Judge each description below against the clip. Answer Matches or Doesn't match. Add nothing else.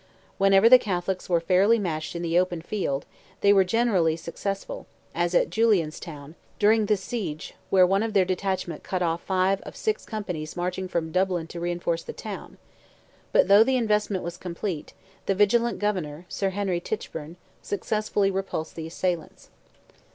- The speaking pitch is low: Doesn't match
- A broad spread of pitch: Doesn't match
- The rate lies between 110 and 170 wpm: Matches